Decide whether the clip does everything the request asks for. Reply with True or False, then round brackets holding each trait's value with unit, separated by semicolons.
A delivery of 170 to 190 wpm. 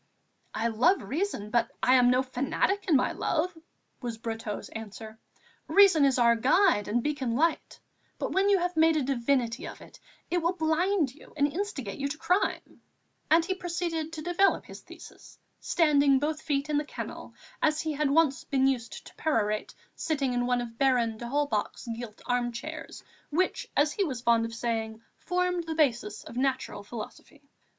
True (175 wpm)